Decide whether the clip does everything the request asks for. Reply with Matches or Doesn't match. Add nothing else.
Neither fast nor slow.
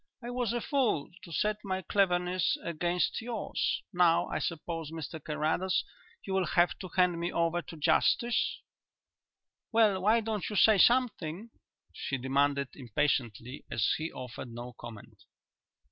Matches